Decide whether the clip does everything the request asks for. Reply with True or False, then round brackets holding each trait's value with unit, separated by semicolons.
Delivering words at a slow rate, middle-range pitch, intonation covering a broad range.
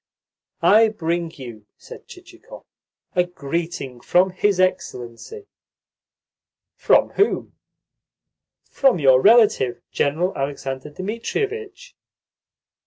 True (85 wpm; 175 Hz; 7.9 semitones)